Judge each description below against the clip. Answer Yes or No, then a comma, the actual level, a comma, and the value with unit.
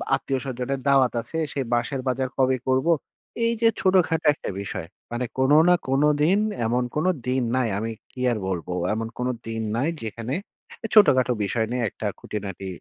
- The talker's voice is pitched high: No, low, 130 Hz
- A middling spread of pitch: Yes, average, 3.1 semitones